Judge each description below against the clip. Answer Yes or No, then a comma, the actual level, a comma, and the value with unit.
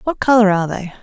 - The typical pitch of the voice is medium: No, high, 210 Hz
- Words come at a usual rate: No, fast, 235 wpm